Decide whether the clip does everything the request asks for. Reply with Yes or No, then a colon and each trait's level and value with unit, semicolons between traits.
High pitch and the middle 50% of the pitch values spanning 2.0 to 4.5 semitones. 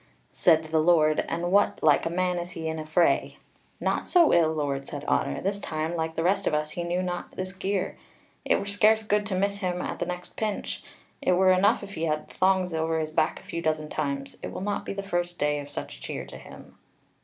No: medium, 175 Hz; average, 3.3 semitones